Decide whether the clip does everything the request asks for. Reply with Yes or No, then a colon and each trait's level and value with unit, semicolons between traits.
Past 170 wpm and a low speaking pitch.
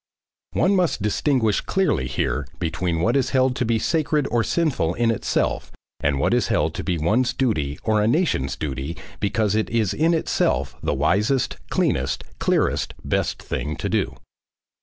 No: average, 165 wpm; low, 110 Hz